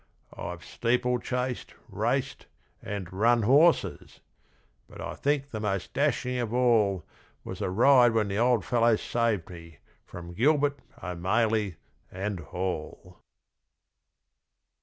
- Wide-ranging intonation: No, average, 4.7 semitones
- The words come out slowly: Yes, slow, 115 wpm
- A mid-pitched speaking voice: No, low, 115 Hz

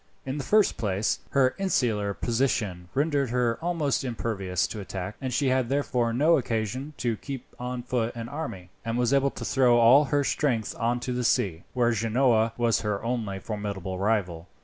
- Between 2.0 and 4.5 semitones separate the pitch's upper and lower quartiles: Yes, average, 3.8 semitones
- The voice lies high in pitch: No, low, 120 Hz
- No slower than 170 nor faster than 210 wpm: Yes, average, 180 wpm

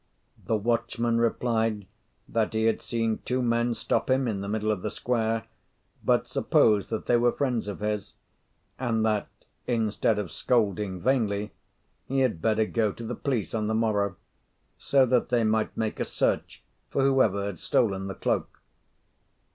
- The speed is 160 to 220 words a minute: Yes, average, 165 wpm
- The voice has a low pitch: Yes, low, 110 Hz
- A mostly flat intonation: Yes, narrow, 2.2 semitones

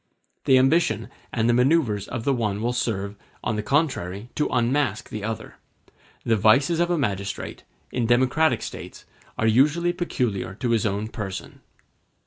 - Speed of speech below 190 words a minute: Yes, average, 155 wpm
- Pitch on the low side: Yes, low, 120 Hz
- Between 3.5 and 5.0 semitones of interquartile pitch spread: Yes, average, 4.6 semitones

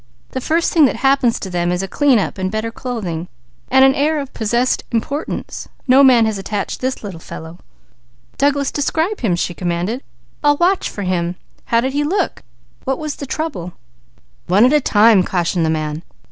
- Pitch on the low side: No, high, 235 Hz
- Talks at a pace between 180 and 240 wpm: Yes, average, 185 wpm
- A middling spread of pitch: No, wide, 7.1 semitones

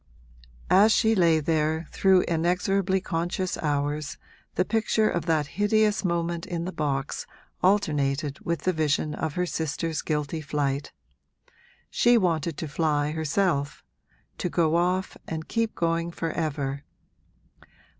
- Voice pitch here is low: No, medium, 165 Hz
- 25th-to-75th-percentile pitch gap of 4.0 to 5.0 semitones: No, average, 3.5 semitones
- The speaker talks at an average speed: No, slow, 130 wpm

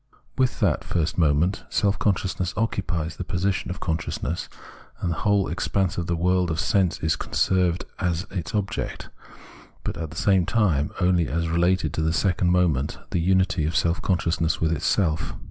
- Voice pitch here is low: Yes, very low, 90 Hz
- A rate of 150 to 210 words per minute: Yes, average, 170 wpm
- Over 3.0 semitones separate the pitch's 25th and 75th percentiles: No, narrow, 2.5 semitones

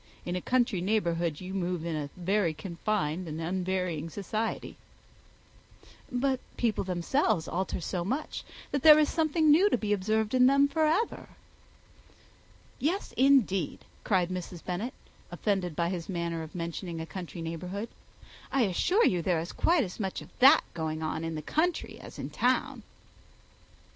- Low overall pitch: No, medium, 185 Hz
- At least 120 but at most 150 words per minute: No, average, 160 wpm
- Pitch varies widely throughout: Yes, wide, 6.7 semitones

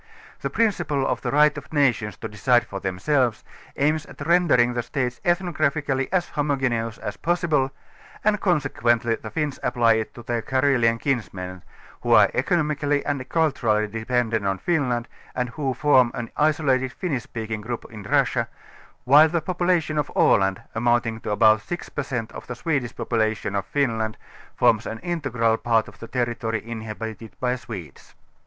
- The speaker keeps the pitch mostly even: No, average, 4.6 semitones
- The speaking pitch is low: Yes, low, 125 Hz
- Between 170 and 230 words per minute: Yes, average, 175 wpm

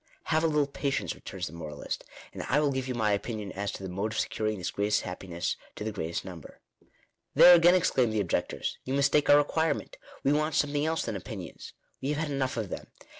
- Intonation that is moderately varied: No, wide, 6.7 semitones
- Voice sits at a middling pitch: No, low, 120 Hz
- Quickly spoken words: Yes, fast, 235 wpm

